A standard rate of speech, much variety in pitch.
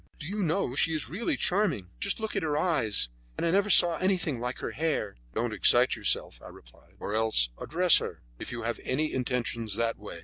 No: fast, 210 wpm; wide, 8.0 semitones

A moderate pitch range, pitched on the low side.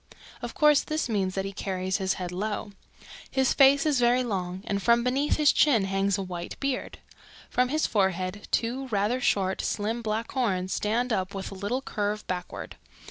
No: average, 4.7 semitones; high, 210 Hz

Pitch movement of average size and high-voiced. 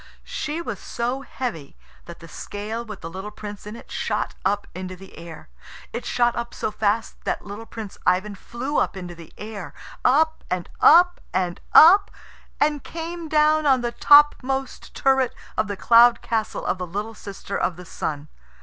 No: wide, 5.9 semitones; high, 220 Hz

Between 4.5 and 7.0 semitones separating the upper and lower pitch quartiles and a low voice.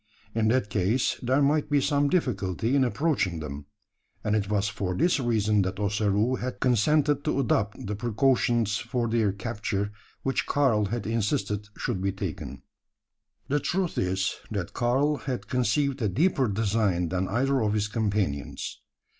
Yes: average, 4.8 semitones; low, 110 Hz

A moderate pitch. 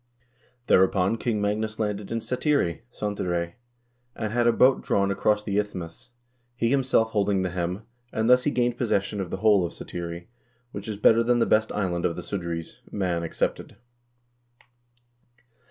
No: low, 105 Hz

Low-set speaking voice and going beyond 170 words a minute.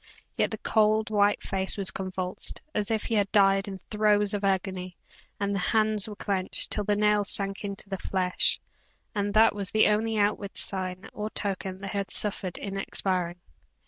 No: high, 200 Hz; average, 180 wpm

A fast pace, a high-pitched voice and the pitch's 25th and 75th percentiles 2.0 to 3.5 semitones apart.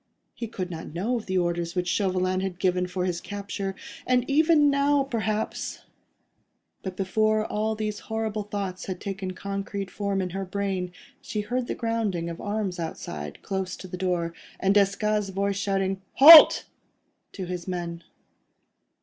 No: average, 160 wpm; high, 195 Hz; average, 2.8 semitones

